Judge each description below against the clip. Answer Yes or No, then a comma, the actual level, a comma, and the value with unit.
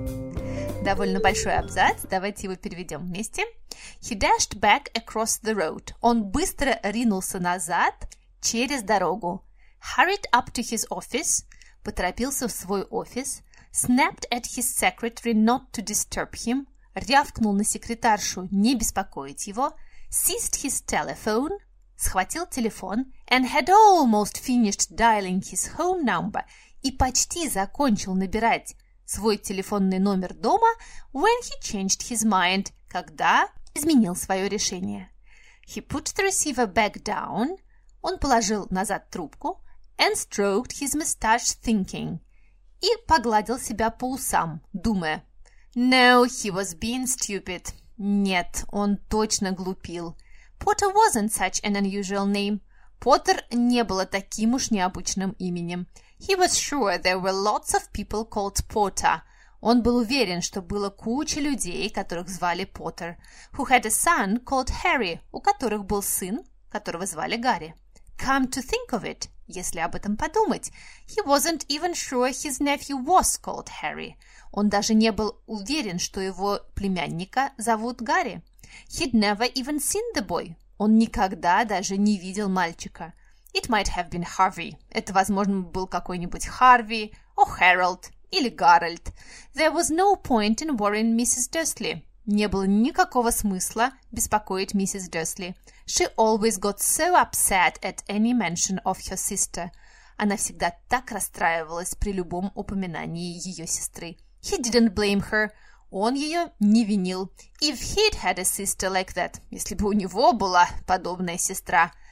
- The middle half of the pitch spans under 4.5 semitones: No, average, 4.9 semitones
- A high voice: Yes, high, 215 Hz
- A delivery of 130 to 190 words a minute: Yes, average, 140 wpm